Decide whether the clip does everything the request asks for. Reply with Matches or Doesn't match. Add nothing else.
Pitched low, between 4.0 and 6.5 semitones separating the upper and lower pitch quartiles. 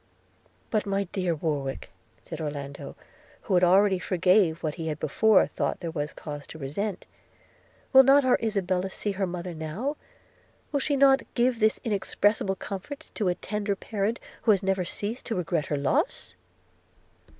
Doesn't match